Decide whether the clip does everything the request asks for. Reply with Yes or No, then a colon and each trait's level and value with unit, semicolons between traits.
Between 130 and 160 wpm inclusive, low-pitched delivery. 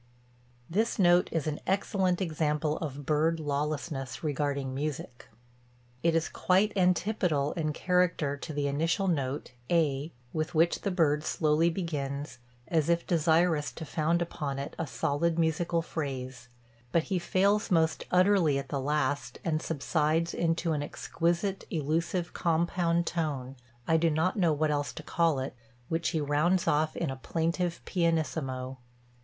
No: average, 150 wpm; medium, 160 Hz